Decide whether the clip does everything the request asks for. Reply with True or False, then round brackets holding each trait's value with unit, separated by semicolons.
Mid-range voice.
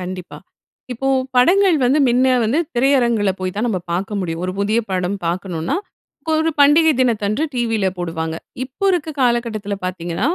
False (220 Hz)